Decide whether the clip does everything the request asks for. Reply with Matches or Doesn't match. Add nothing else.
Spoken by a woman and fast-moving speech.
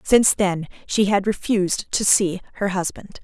Doesn't match